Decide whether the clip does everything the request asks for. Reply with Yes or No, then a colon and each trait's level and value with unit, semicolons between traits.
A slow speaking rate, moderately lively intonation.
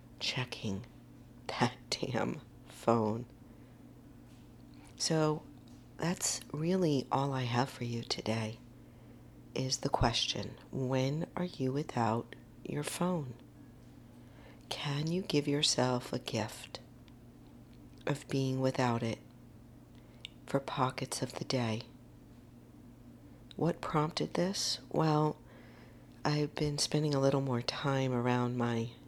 Yes: slow, 105 wpm; average, 3.9 semitones